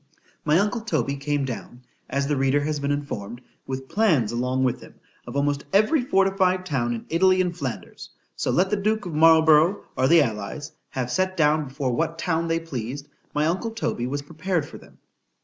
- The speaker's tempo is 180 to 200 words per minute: Yes, average, 190 wpm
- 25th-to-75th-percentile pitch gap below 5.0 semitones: No, wide, 5.4 semitones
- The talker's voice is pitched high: No, medium, 150 Hz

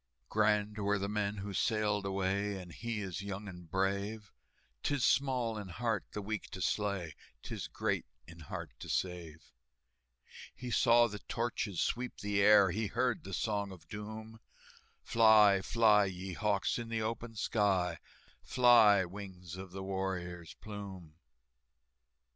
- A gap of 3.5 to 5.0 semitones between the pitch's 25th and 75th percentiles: No, narrow, 2.5 semitones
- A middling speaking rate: Yes, average, 145 wpm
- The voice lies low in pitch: Yes, low, 100 Hz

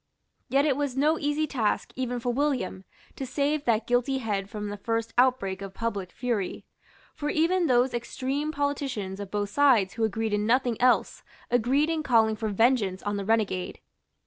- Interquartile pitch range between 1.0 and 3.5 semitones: No, average, 4.9 semitones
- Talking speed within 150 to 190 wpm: Yes, average, 175 wpm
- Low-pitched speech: No, high, 240 Hz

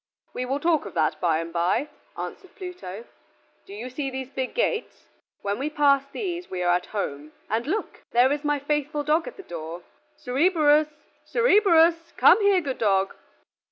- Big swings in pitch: Yes, wide, 8.6 semitones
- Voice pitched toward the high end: Yes, very high, 280 Hz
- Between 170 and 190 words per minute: Yes, average, 175 wpm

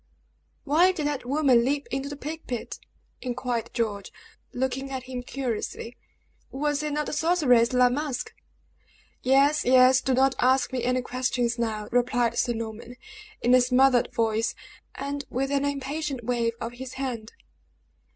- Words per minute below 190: Yes, average, 150 wpm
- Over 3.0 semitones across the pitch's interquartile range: No, narrow, 2.5 semitones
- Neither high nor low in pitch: No, very high, 255 Hz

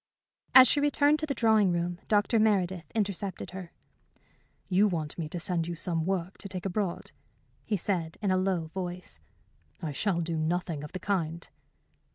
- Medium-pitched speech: Yes, medium, 180 Hz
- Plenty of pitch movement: No, average, 3.3 semitones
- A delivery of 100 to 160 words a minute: No, average, 175 wpm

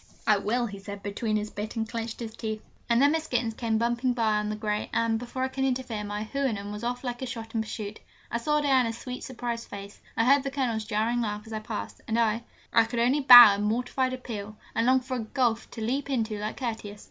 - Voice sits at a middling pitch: No, high, 230 Hz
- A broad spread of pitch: No, average, 2.7 semitones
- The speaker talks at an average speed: No, fast, 240 wpm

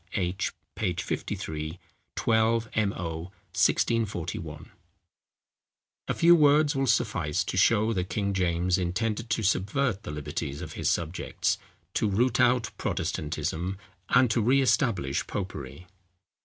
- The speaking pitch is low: Yes, low, 100 Hz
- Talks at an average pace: No, slow, 115 wpm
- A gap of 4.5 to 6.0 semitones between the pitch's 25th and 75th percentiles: Yes, average, 4.9 semitones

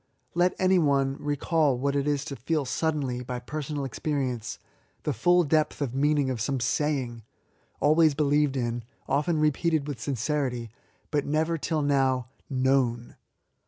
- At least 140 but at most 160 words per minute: Yes, average, 155 wpm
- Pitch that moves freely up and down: No, average, 2.8 semitones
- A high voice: No, medium, 140 Hz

